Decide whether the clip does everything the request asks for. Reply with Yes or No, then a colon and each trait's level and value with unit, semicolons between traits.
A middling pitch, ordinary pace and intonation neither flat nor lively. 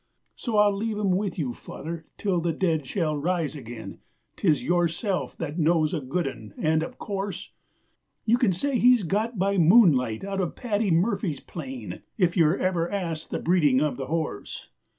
Yes: medium, 175 Hz; average, 175 wpm; average, 4.4 semitones